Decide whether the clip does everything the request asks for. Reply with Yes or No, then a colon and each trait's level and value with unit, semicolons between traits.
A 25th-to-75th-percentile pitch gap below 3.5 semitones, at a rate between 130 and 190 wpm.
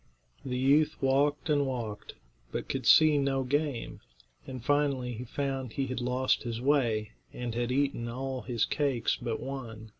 Yes: average, 2.7 semitones; average, 170 wpm